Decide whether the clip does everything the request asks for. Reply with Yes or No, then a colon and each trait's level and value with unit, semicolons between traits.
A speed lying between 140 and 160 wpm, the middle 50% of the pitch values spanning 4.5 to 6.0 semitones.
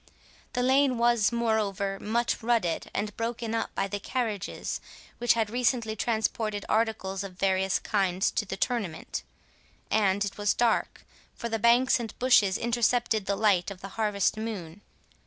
No: average, 155 wpm; average, 3.0 semitones